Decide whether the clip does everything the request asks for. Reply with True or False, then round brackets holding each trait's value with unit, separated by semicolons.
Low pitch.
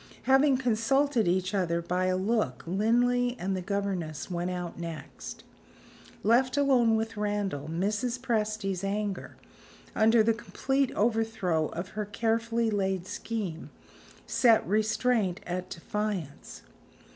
False (210 Hz)